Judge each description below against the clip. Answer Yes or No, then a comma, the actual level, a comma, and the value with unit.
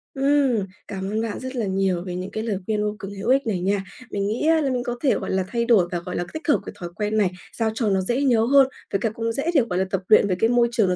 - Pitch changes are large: No, average, 4.0 semitones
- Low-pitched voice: No, high, 220 Hz